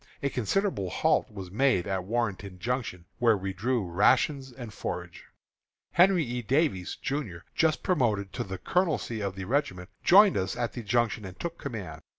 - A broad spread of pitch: Yes, wide, 6.2 semitones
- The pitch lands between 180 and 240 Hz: No, low, 115 Hz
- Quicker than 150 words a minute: Yes, average, 165 wpm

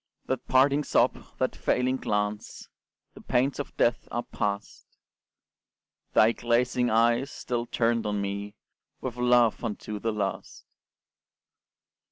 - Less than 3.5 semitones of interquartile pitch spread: Yes, average, 2.8 semitones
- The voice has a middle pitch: No, low, 120 Hz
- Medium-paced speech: No, slow, 120 wpm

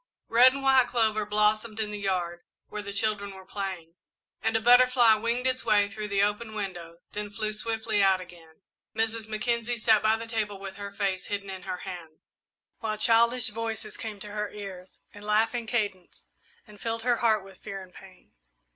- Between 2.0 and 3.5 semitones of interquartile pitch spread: Yes, narrow, 2.4 semitones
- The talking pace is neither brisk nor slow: Yes, average, 190 wpm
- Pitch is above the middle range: Yes, high, 210 Hz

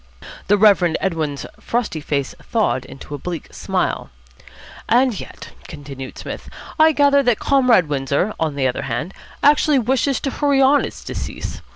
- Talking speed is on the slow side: No, average, 155 wpm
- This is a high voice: Yes, high, 205 Hz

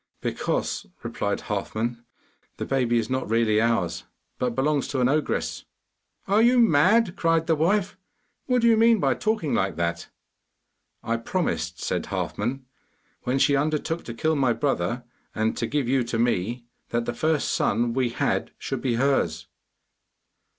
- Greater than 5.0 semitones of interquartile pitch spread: Yes, wide, 5.5 semitones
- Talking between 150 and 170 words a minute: Yes, average, 155 wpm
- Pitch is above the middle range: No, low, 130 Hz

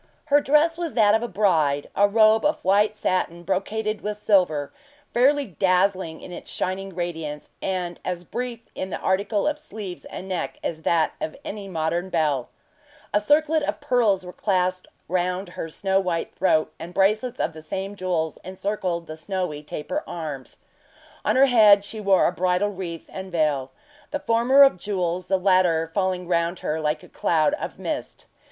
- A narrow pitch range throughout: No, average, 3.7 semitones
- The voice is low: No, medium, 185 Hz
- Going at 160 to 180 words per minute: Yes, average, 175 wpm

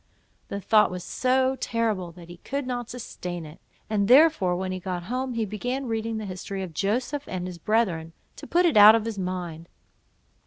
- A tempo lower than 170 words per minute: No, average, 195 wpm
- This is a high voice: Yes, high, 210 Hz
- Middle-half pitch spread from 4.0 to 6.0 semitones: Yes, average, 5.2 semitones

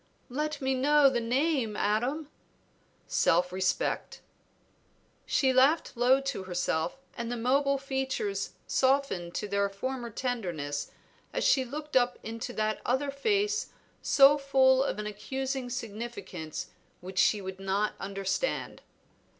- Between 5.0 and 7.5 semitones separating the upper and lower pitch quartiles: Yes, average, 5.3 semitones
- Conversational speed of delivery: No, slow, 125 wpm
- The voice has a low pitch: No, very high, 250 Hz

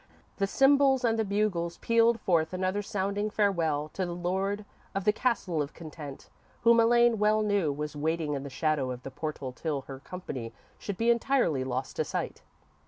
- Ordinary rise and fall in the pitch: No, wide, 6.1 semitones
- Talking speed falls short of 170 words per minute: No, average, 180 wpm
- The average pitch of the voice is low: No, medium, 185 Hz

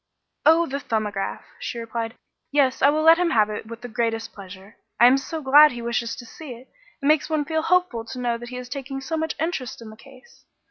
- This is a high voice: Yes, very high, 255 Hz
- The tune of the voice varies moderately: Yes, average, 4.7 semitones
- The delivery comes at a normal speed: No, fast, 235 wpm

